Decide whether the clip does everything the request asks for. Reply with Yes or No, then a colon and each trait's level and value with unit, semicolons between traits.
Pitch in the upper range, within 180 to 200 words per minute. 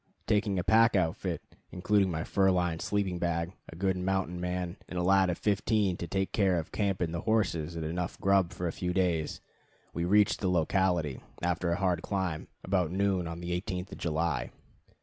No: very low, 90 Hz; average, 195 wpm